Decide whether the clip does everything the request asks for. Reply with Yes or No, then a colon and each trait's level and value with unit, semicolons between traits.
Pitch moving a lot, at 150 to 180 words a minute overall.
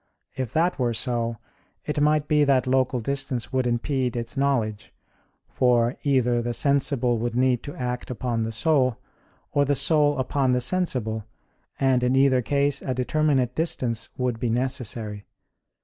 No: average, 2.8 semitones; average, 155 wpm